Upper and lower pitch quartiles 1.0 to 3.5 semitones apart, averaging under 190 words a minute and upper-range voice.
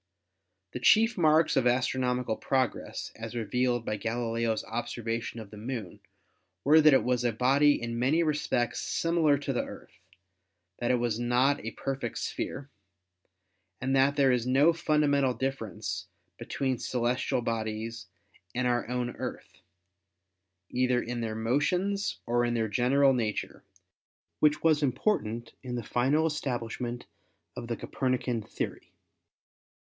No: average, 3.1 semitones; average, 140 wpm; low, 125 Hz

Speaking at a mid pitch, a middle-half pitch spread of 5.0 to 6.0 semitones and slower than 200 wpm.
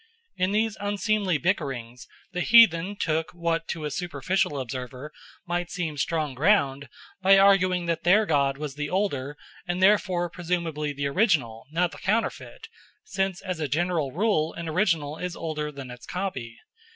No: medium, 170 Hz; average, 4.4 semitones; average, 155 wpm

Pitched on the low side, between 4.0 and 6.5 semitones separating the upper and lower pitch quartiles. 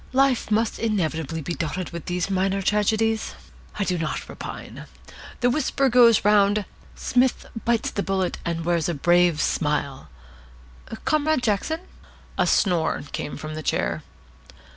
No: high, 195 Hz; average, 5.1 semitones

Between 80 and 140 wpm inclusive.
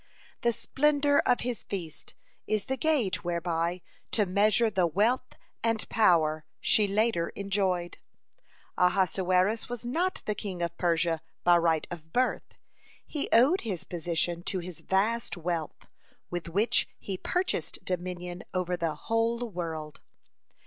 Yes: slow, 135 wpm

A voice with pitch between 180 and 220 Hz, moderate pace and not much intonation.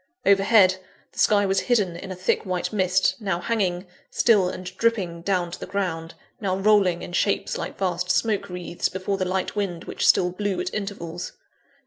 Yes: high, 190 Hz; average, 180 wpm; narrow, 2.0 semitones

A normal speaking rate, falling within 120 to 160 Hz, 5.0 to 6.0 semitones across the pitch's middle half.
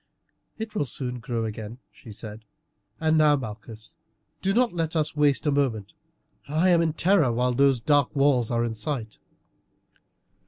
Yes: average, 160 wpm; low, 135 Hz; average, 5.3 semitones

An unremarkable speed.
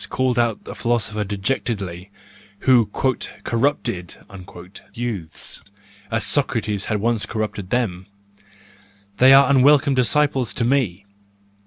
No: slow, 100 wpm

